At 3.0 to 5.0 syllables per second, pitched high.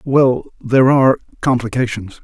No: 4.9 syllables/s; low, 125 Hz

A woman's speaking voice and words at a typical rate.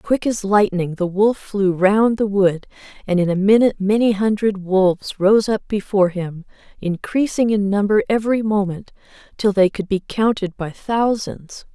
Yes: female; average, 165 wpm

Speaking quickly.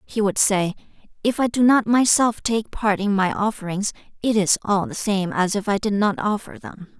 Yes: fast, 215 wpm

